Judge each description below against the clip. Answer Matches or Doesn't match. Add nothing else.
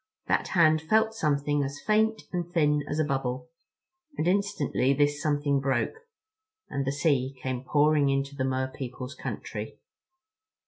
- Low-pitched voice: Doesn't match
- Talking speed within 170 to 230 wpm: Doesn't match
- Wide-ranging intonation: Doesn't match